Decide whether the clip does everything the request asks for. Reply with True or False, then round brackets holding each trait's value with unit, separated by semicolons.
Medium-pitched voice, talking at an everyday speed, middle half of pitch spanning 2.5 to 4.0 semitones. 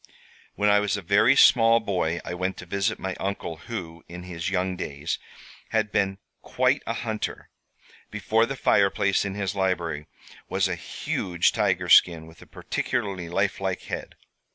False (95 Hz; 160 wpm; 2.8 semitones)